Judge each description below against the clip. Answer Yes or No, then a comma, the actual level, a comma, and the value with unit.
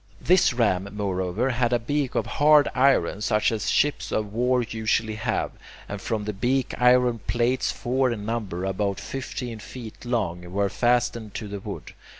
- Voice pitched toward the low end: Yes, low, 115 Hz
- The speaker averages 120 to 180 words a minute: Yes, average, 165 wpm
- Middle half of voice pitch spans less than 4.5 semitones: Yes, average, 3.3 semitones